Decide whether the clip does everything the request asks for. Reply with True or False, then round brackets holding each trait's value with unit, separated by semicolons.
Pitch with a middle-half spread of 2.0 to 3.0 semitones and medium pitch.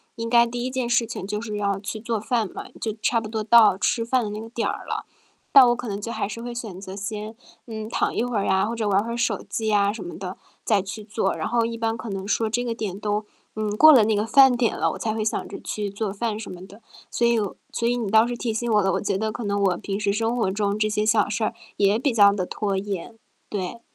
False (2.4 semitones; 215 Hz)